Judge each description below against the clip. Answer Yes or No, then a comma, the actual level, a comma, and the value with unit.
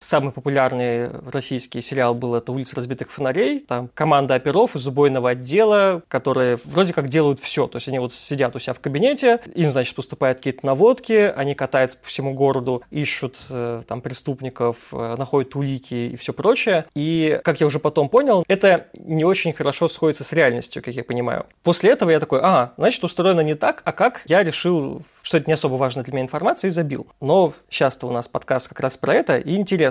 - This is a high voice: No, medium, 140 Hz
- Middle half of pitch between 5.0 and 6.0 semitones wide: No, average, 4.0 semitones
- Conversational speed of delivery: No, fast, 195 wpm